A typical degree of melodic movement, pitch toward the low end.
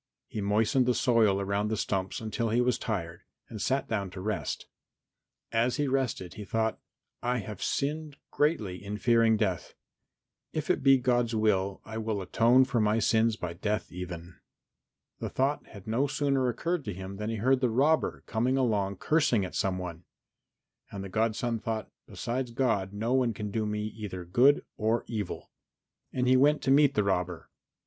Yes: average, 4.0 semitones; low, 110 Hz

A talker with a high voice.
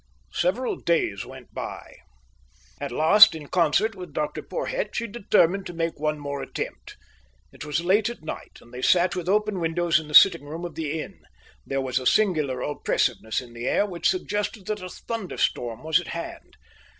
No: medium, 170 Hz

